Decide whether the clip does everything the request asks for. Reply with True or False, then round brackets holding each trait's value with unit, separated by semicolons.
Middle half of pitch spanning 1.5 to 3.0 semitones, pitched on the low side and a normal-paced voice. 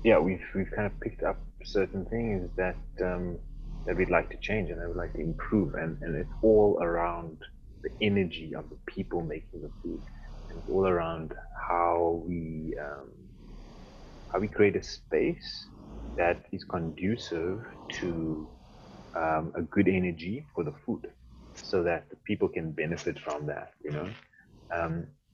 True (2.4 semitones; 85 Hz; 165 wpm)